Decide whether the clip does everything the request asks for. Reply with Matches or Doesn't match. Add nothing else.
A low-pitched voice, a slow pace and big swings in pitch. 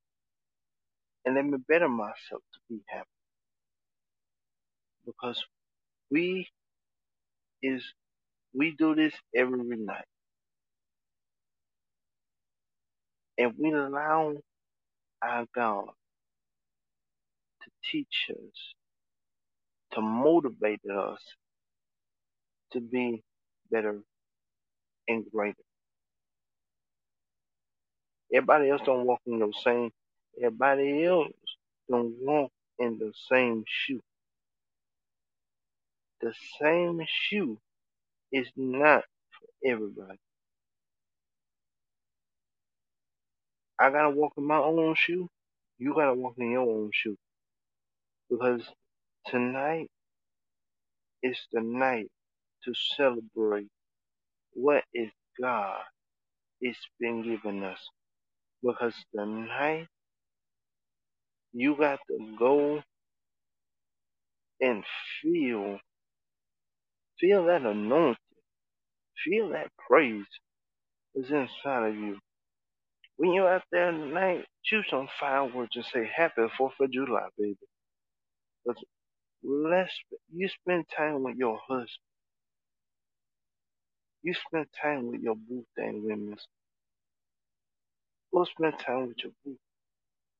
Matches